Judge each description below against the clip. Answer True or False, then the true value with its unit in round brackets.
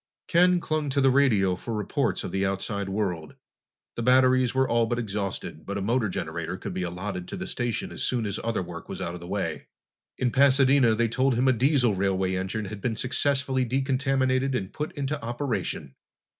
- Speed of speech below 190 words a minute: False (200 wpm)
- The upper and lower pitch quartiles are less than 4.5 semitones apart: False (5.3 semitones)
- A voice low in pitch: True (120 Hz)